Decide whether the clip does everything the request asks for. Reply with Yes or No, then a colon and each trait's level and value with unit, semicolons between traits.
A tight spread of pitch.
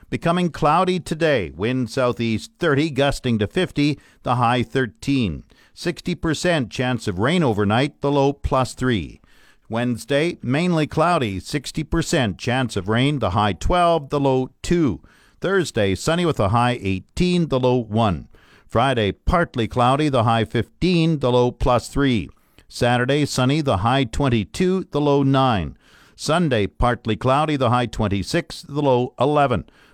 No: average, 4.9 semitones